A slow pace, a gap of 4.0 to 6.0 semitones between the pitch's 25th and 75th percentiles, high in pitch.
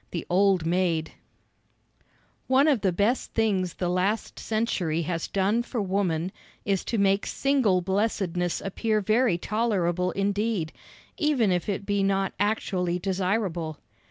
No: slow, 130 wpm; average, 3.3 semitones; high, 195 Hz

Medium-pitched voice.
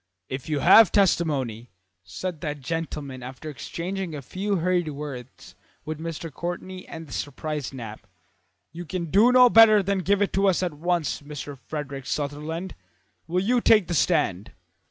Yes: medium, 160 Hz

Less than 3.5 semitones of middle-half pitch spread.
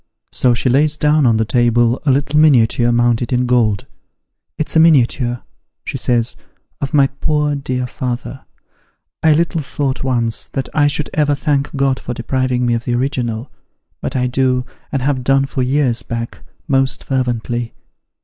Yes: average, 2.7 semitones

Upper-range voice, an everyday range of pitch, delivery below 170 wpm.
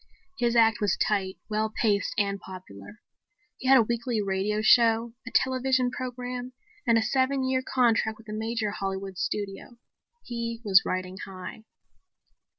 Yes: high, 225 Hz; average, 3.6 semitones; average, 150 wpm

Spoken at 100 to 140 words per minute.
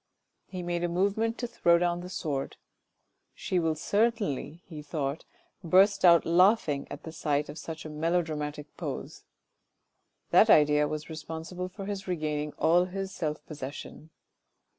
No: average, 160 wpm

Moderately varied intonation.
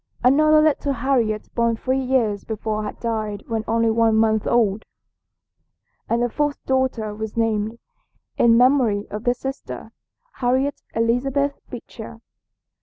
Yes: average, 3.1 semitones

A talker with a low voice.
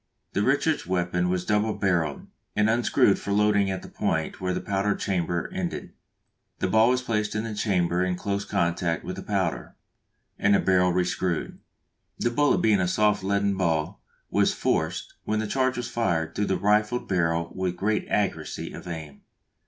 Yes: low, 100 Hz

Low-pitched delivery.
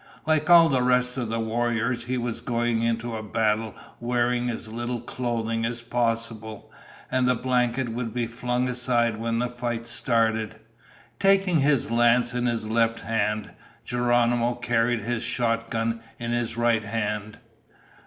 Yes: low, 120 Hz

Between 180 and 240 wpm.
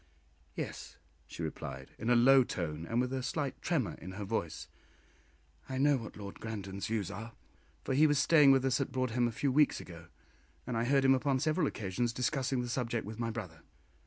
Yes: average, 200 wpm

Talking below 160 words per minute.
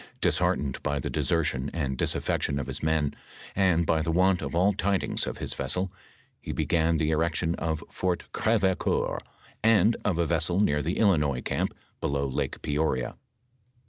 No: average, 165 wpm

